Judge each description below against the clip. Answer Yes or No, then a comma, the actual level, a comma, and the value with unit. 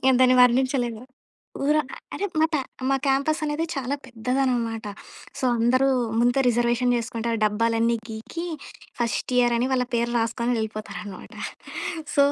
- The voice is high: Yes, high, 240 Hz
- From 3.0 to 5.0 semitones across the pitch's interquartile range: No, narrow, 2.5 semitones